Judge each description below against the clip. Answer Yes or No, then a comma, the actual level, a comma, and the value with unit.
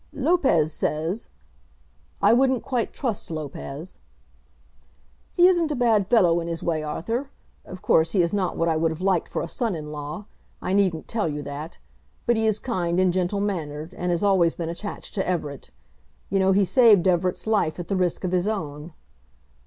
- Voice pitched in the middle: Yes, medium, 180 Hz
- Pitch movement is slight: No, average, 4.6 semitones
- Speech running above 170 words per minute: Yes, average, 190 wpm